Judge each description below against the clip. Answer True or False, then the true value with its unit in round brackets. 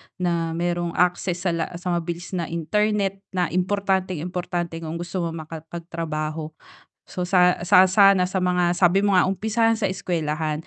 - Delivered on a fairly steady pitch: True (1.9 semitones)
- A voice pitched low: False (180 Hz)